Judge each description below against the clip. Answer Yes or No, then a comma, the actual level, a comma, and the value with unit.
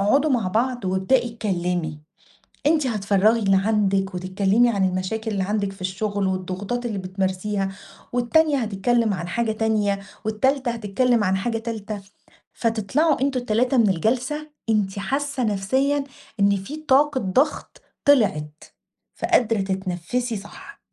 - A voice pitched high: Yes, high, 215 Hz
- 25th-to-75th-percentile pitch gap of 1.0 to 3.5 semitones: No, average, 4.2 semitones